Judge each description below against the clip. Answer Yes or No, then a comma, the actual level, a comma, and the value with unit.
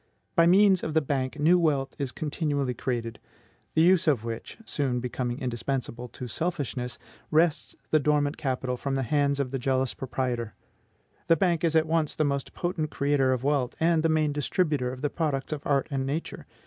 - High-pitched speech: No, medium, 140 Hz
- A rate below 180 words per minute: No, average, 185 wpm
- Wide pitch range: No, average, 3.5 semitones